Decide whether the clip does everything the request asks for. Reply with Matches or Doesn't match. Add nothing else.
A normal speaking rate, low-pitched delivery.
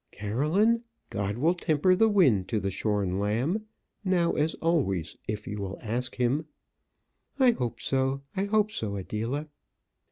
Matches